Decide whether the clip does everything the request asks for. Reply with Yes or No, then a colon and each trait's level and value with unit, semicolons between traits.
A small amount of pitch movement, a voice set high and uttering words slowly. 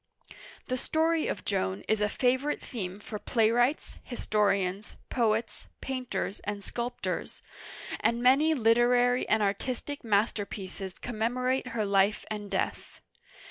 No: average, 3.5 semitones; high, 230 Hz; slow, 115 wpm